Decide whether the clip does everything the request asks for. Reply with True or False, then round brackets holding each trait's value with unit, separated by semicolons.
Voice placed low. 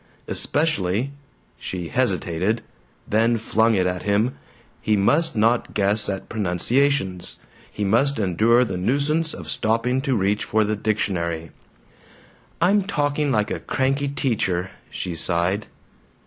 True (110 Hz)